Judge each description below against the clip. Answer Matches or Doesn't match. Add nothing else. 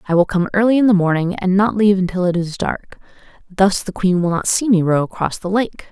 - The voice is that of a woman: Matches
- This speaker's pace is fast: Matches